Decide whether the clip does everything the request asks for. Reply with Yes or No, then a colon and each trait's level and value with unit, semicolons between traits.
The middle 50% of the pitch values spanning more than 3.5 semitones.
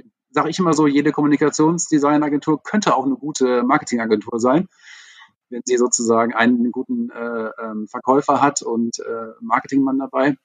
Yes: average, 4.1 semitones